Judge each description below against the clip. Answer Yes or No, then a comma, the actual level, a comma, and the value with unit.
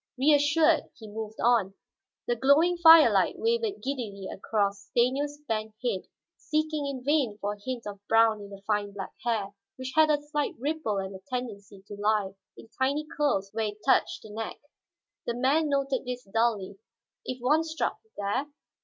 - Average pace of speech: Yes, average, 170 wpm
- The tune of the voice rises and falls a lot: Yes, wide, 5.9 semitones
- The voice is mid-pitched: No, high, 240 Hz